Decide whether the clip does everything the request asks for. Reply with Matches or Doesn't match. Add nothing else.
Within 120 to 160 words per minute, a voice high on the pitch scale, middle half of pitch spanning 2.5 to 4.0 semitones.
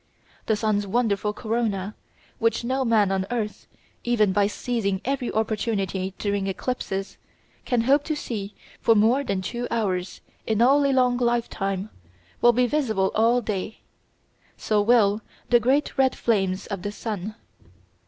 Matches